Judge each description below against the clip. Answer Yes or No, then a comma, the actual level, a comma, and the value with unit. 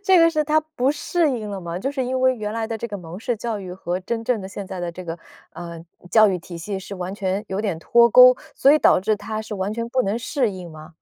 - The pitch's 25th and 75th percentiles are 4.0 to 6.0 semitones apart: Yes, average, 5.1 semitones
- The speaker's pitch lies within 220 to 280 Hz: No, high, 210 Hz